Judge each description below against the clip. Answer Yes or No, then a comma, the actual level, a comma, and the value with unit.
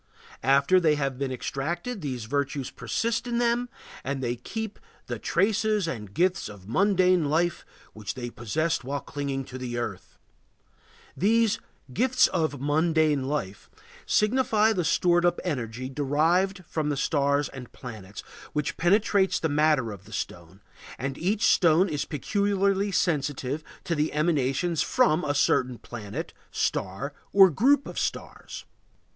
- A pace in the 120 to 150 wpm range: Yes, average, 140 wpm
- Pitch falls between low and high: Yes, medium, 150 Hz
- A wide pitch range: Yes, wide, 6.2 semitones